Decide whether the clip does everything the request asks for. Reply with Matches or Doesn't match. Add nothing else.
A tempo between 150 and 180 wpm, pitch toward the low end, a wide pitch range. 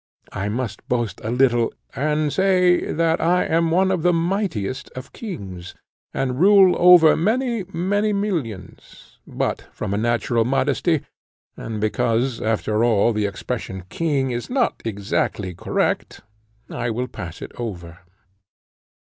Doesn't match